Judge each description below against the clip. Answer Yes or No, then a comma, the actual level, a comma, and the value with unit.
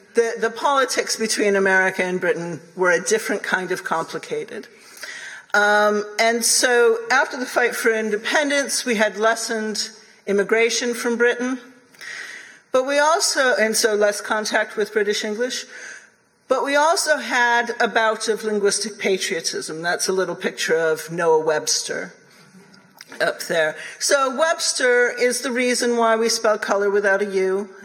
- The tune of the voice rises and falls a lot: No, average, 3.3 semitones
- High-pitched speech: Yes, high, 220 Hz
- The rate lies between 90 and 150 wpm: Yes, average, 145 wpm